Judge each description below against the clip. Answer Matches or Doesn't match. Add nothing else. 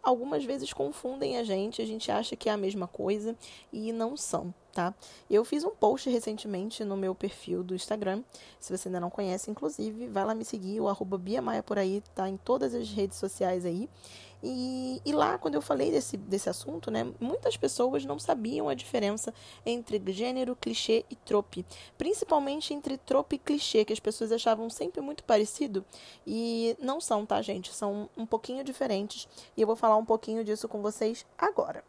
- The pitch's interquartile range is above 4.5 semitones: Doesn't match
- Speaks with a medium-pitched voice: Doesn't match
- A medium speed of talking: Doesn't match